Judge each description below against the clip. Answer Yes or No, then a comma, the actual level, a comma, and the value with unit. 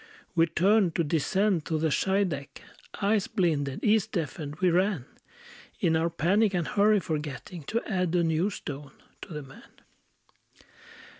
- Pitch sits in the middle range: Yes, medium, 170 Hz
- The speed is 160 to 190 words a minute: No, average, 145 wpm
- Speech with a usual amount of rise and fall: Yes, average, 4.3 semitones